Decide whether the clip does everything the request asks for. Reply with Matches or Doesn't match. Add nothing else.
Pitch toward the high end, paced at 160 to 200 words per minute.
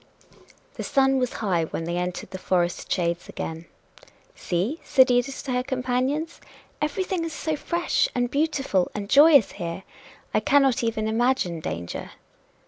Doesn't match